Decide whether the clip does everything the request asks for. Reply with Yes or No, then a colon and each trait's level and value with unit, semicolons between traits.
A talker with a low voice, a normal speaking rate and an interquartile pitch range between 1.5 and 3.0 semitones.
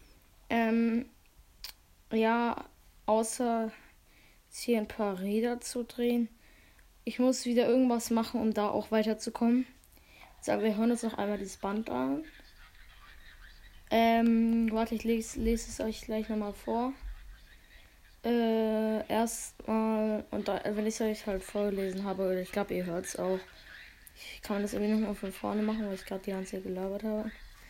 No: high, 220 Hz; average, 165 wpm; narrow, 2.6 semitones